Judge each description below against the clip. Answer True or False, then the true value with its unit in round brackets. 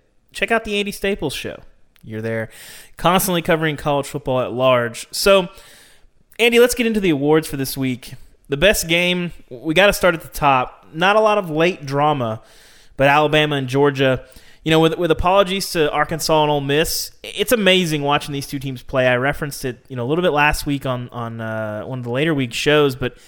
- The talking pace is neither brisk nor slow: False (210 wpm)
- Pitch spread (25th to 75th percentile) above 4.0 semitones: True (5.2 semitones)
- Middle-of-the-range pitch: True (150 Hz)